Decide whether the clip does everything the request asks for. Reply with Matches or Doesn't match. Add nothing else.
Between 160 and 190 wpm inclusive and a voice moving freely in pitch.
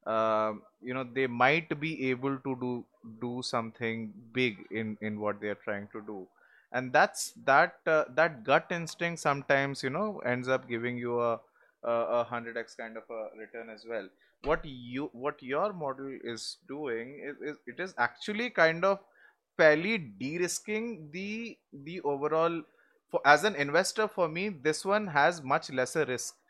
Matches